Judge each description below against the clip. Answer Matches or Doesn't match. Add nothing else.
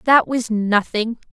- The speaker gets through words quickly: Doesn't match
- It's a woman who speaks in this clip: Matches